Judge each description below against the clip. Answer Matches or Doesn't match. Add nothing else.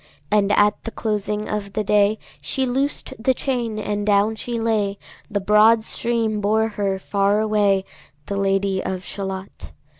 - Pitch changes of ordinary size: Doesn't match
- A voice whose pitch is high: Matches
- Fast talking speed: Doesn't match